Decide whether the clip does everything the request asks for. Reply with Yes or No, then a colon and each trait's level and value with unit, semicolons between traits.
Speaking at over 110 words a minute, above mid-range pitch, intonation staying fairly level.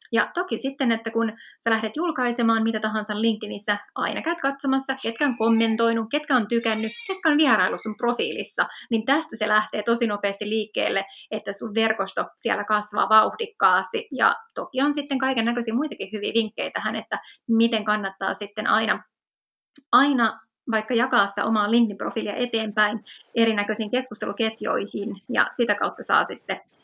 No: average, 150 wpm; high, 225 Hz; average, 3.1 semitones